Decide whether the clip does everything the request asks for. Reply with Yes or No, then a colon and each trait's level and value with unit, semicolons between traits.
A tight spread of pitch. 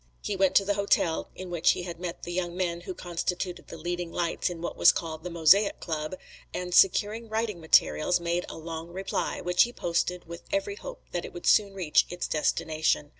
Yes: narrow, 2.3 semitones